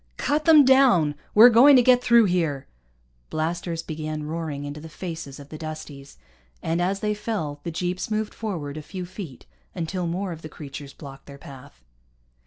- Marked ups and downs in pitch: Yes, wide, 5.7 semitones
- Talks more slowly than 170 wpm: No, average, 180 wpm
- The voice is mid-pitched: Yes, medium, 165 Hz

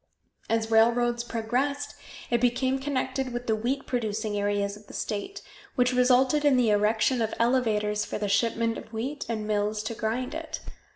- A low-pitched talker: No, high, 235 Hz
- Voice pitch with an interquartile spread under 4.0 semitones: Yes, average, 3.0 semitones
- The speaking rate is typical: Yes, average, 170 wpm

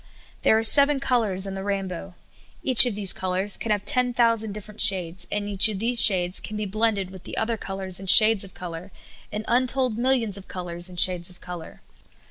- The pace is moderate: No, fast, 210 wpm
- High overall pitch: Yes, high, 205 Hz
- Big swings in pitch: No, average, 3.3 semitones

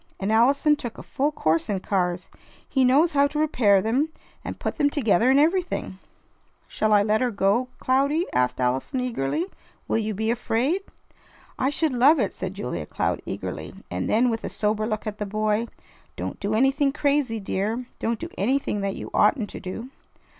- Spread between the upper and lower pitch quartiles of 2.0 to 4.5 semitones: No, average, 5.2 semitones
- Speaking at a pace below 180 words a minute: No, average, 185 wpm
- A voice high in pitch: Yes, high, 230 Hz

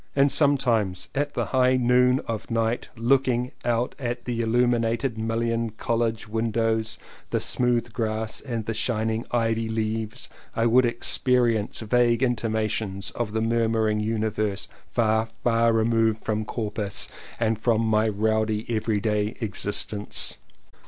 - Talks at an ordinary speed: No, slow, 130 wpm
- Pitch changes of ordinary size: No, narrow, 1.5 semitones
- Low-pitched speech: Yes, low, 115 Hz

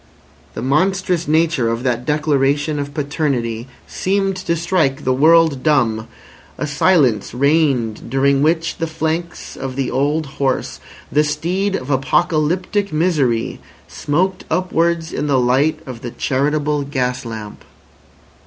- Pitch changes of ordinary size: Yes, average, 4.0 semitones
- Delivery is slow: Yes, slow, 130 wpm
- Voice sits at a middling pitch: Yes, medium, 150 Hz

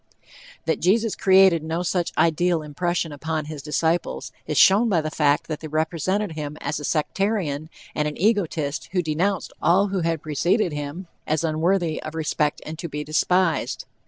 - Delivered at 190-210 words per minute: No, average, 170 wpm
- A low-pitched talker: No, medium, 160 Hz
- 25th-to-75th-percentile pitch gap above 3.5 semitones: No, average, 3.1 semitones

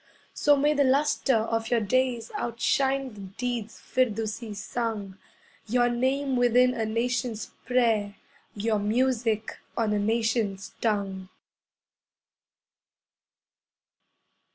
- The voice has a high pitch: Yes, high, 230 Hz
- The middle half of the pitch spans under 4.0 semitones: Yes, average, 3.0 semitones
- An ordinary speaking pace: No, slow, 100 wpm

